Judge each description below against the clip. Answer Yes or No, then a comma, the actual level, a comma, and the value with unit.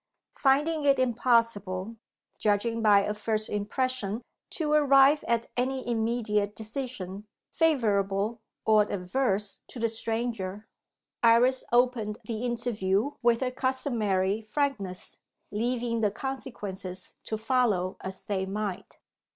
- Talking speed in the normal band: No, slow, 110 wpm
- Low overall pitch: No, high, 225 Hz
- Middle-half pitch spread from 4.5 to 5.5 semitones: No, average, 3.7 semitones